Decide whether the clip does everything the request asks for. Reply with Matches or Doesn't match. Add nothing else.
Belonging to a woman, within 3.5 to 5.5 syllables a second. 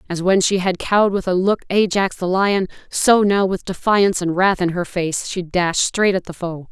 Matches